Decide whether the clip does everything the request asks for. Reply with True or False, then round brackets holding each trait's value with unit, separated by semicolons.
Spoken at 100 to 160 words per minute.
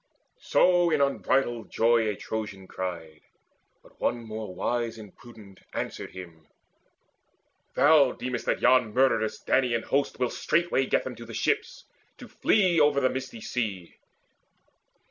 True (140 wpm)